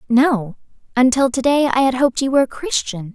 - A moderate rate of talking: No, fast, 210 wpm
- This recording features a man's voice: No, female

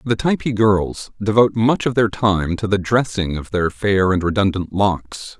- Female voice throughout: No, male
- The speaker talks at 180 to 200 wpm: Yes, average, 190 wpm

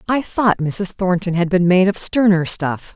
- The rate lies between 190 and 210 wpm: Yes, fast, 205 wpm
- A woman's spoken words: Yes, female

